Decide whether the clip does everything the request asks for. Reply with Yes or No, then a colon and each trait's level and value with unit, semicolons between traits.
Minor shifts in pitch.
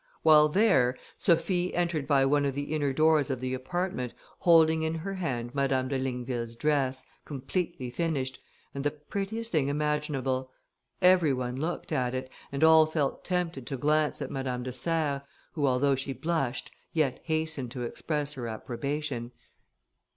No: average, 3.6 semitones